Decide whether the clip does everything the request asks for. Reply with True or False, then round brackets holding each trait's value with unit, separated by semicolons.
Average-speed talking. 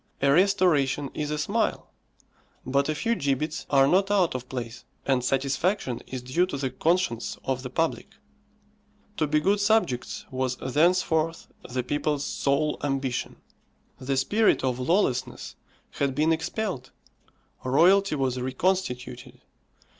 False (130 wpm)